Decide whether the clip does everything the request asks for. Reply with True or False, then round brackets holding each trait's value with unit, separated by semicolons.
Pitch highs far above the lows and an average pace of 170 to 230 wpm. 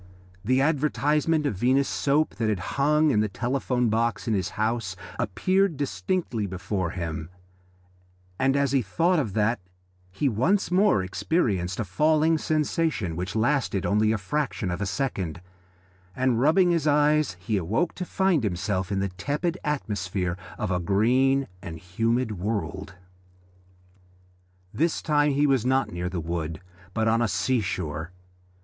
False (7.4 semitones; 150 wpm)